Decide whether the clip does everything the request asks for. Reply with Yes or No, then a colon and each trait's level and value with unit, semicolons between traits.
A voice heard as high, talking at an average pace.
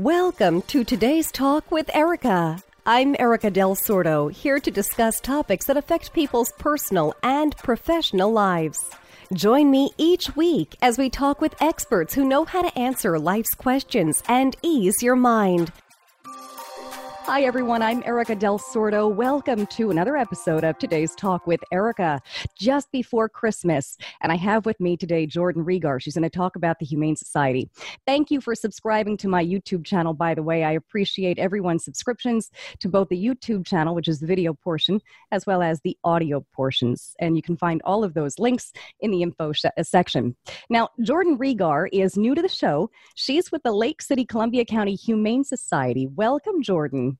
Yes: high, 210 Hz; average, 175 wpm